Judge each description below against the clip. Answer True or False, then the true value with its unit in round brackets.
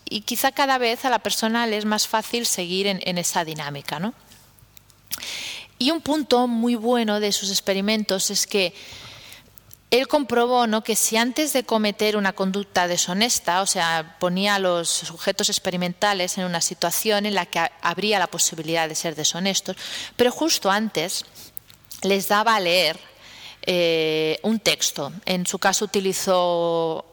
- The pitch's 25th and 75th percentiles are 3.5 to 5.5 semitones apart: True (4.2 semitones)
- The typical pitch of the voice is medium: False (195 Hz)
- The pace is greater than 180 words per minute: False (160 wpm)